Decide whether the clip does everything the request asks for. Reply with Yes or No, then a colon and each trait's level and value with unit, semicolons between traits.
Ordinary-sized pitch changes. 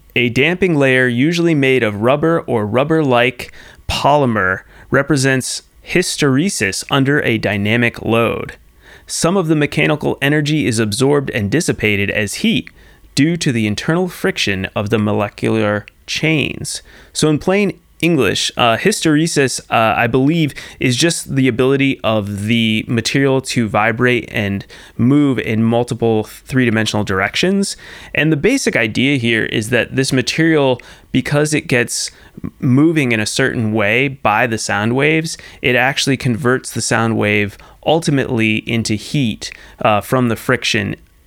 Yes: average, 4.9 semitones